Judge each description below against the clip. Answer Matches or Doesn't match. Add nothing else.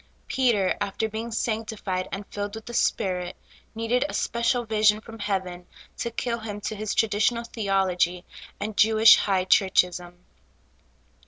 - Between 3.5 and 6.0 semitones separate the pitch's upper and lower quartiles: Doesn't match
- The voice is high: Matches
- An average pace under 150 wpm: Matches